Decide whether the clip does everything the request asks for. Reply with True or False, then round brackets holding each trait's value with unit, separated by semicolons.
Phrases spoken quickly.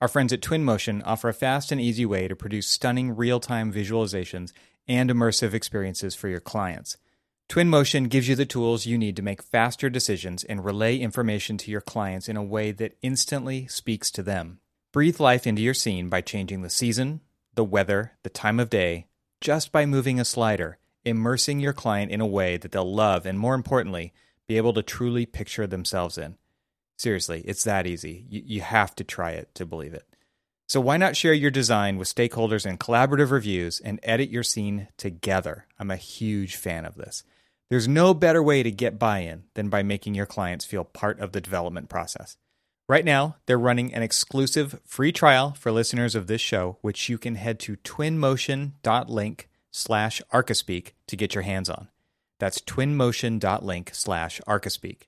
False (185 wpm)